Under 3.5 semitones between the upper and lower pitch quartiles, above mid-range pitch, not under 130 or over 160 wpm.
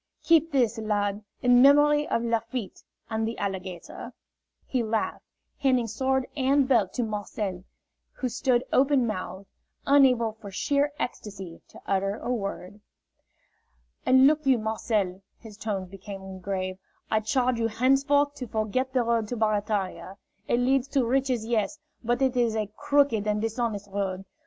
No: average, 4.2 semitones; high, 225 Hz; average, 150 wpm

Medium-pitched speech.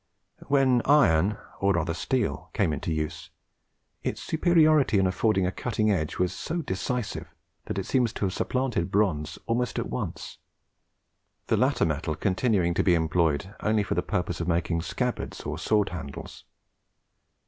No: very low, 95 Hz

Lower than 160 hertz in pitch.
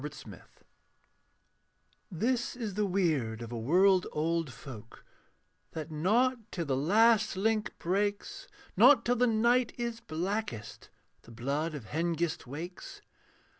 No: medium, 180 Hz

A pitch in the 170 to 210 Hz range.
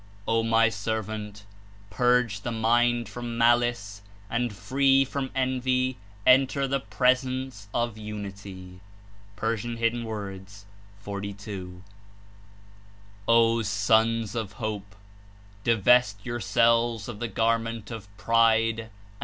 No: low, 115 Hz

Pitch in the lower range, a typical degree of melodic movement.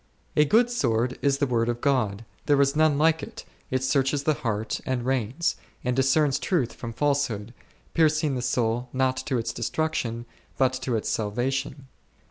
Yes: low, 130 Hz; average, 3.4 semitones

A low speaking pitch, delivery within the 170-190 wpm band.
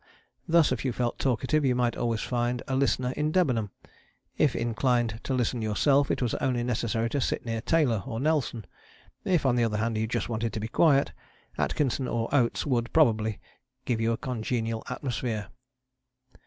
Yes: low, 120 Hz; average, 180 wpm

